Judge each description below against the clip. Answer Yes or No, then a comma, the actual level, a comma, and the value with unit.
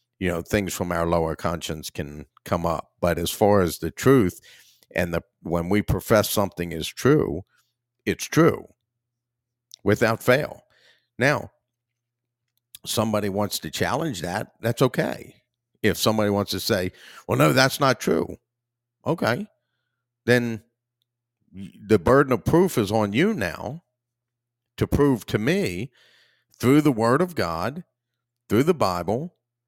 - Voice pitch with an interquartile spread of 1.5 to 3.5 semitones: Yes, average, 2.9 semitones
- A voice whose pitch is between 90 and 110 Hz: No, low, 120 Hz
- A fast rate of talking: No, average, 140 wpm